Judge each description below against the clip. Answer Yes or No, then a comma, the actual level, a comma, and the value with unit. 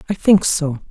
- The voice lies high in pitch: No, medium, 170 Hz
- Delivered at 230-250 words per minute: No, average, 200 wpm